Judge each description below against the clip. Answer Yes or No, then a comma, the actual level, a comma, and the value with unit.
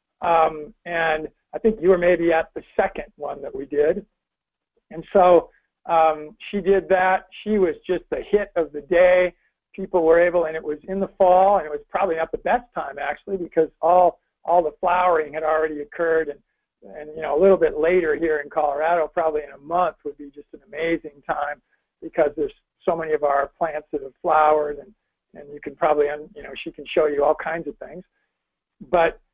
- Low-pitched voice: No, medium, 165 Hz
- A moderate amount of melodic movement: Yes, average, 3.6 semitones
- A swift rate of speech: Yes, fast, 210 wpm